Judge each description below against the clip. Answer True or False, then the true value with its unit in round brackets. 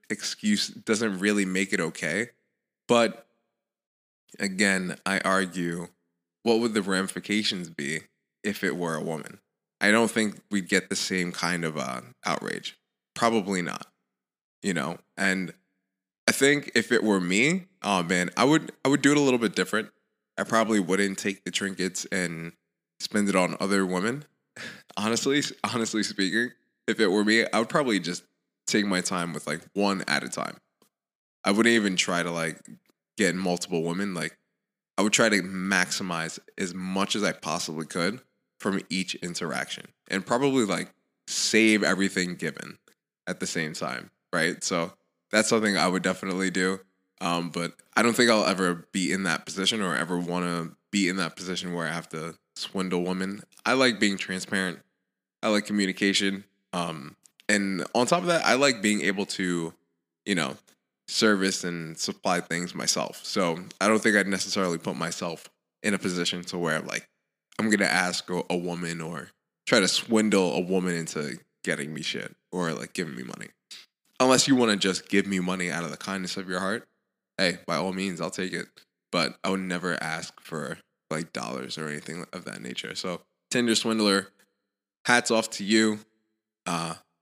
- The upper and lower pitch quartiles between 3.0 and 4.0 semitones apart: True (3.4 semitones)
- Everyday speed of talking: True (175 wpm)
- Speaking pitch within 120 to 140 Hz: False (95 Hz)